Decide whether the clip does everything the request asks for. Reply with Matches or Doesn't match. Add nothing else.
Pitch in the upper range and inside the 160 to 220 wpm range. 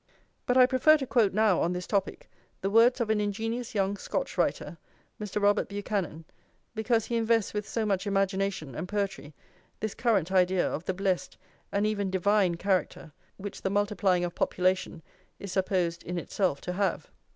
Matches